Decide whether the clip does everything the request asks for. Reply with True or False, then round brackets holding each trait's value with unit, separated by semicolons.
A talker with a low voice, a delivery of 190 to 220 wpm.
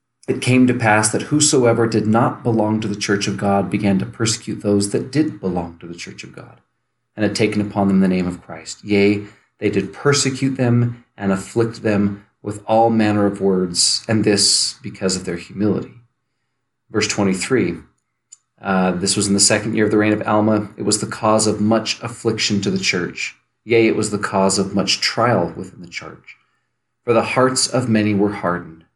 True (105 Hz; 200 wpm)